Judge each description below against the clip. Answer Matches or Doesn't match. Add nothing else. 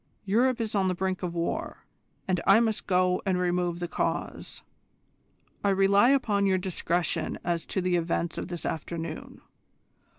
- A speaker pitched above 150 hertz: Matches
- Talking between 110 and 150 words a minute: Doesn't match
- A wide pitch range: Doesn't match